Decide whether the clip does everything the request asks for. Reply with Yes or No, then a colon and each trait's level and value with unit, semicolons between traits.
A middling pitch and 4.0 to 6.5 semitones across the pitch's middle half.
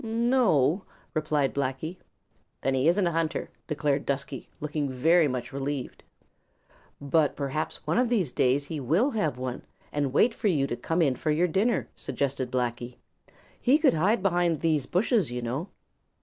Yes: medium, 150 Hz; average, 5.0 semitones